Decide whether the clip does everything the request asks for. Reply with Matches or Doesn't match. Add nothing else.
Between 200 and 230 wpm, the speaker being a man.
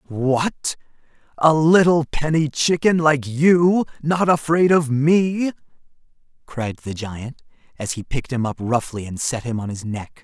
Doesn't match